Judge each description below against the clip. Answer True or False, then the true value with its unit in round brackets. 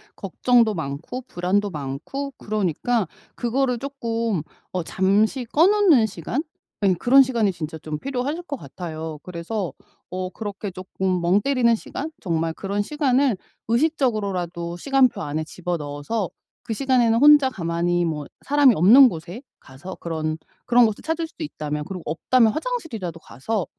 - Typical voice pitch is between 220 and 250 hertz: False (205 Hz)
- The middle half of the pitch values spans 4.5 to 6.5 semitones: False (7.1 semitones)